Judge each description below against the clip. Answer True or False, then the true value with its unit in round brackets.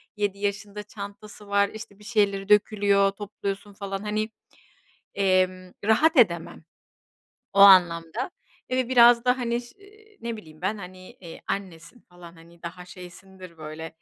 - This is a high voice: True (200 Hz)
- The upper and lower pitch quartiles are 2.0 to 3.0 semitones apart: True (2.7 semitones)